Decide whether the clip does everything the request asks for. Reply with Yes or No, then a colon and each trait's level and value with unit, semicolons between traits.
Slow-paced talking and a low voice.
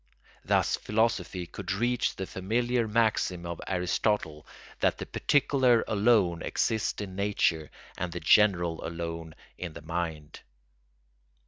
Yes: slow, 120 wpm; very low, 95 Hz